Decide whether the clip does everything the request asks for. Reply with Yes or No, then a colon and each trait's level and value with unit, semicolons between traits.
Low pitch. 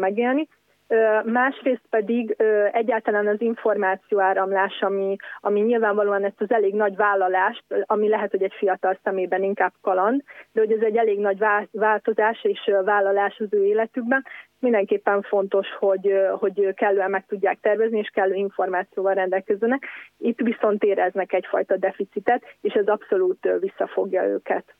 No: high, 210 Hz